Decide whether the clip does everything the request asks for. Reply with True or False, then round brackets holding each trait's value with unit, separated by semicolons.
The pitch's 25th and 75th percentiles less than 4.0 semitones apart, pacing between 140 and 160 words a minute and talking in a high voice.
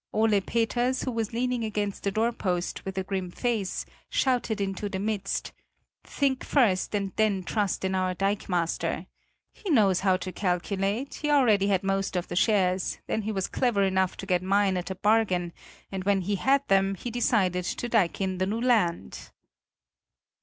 False (3.1 semitones; 175 wpm; 200 Hz)